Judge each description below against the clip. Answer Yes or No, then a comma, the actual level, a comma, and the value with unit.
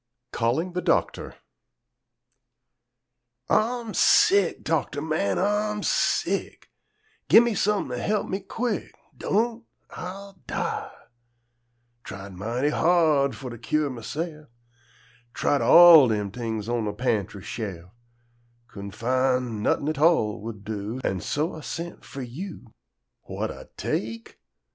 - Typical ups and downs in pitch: No, wide, 8.2 semitones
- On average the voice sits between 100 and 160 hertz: Yes, medium, 140 Hz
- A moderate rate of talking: No, slow, 120 wpm